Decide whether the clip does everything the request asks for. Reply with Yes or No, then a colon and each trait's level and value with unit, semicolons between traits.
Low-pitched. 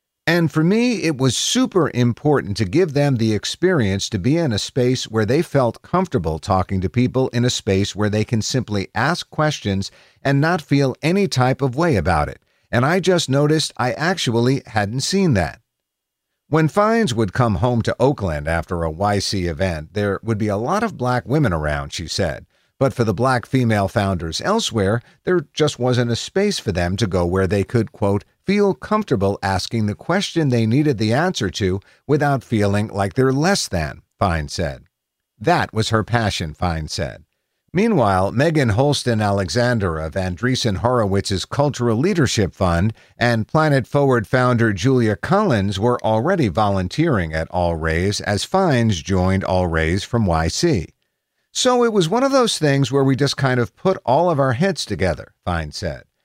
Yes: low, 120 Hz